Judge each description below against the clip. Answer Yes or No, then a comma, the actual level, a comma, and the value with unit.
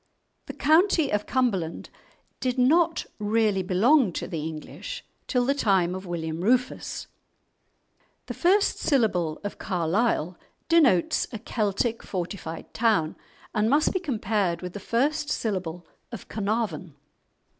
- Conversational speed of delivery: No, slow, 125 wpm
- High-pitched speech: Yes, high, 210 Hz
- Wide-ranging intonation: Yes, wide, 6.2 semitones